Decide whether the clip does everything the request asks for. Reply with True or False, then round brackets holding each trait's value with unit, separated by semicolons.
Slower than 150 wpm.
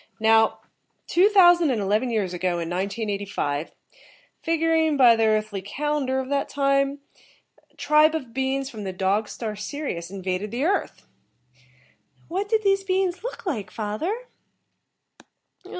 True (140 wpm)